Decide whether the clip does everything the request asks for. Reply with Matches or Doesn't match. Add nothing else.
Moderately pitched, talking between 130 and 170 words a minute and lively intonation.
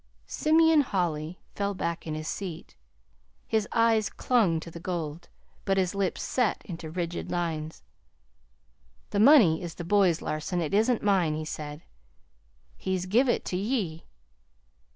Doesn't match